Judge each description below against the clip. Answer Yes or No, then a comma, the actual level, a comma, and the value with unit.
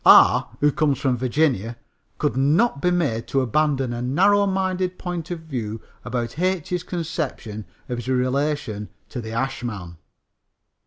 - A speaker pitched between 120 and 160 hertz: Yes, low, 135 Hz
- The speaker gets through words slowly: No, average, 145 wpm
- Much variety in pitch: Yes, wide, 6.0 semitones